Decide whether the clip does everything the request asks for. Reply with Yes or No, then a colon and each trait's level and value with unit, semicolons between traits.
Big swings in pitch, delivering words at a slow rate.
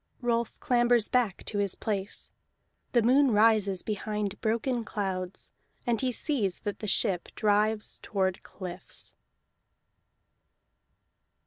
No: average, 3.2 semitones; slow, 110 wpm